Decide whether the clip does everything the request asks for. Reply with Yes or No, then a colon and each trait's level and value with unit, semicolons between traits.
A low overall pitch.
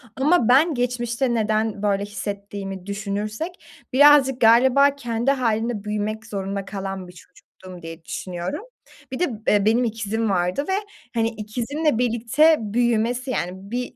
No: high, 225 Hz